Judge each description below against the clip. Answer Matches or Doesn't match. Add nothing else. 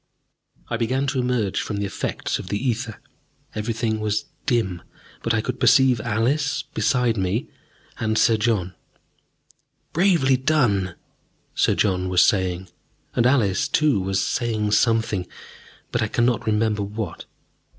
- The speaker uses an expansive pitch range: Doesn't match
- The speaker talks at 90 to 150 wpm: Matches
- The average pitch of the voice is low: Matches